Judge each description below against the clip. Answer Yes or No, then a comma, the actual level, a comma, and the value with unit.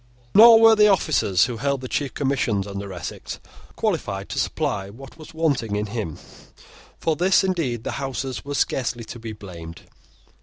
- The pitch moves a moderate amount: No, wide, 7.0 semitones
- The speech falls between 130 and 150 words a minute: No, average, 165 wpm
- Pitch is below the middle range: Yes, low, 125 Hz